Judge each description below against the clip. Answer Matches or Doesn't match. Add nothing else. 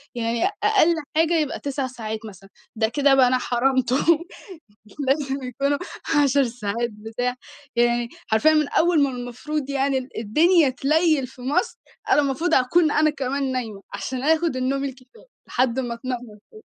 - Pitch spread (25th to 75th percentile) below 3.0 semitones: Doesn't match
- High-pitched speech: Matches